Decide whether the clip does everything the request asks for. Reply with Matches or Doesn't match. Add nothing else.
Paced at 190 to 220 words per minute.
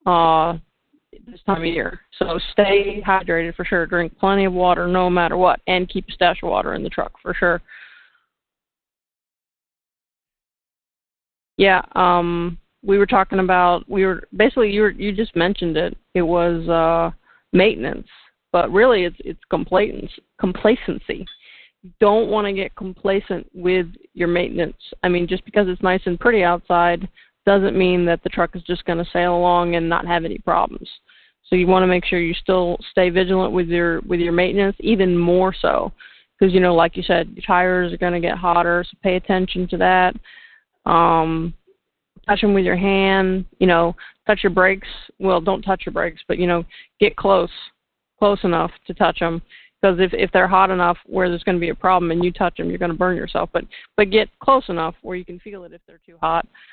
Matches